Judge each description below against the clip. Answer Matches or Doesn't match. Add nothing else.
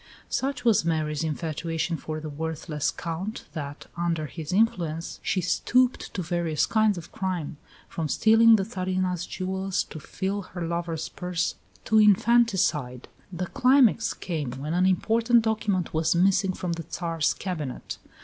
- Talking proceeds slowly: Doesn't match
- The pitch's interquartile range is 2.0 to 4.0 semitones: Matches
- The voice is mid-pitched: Matches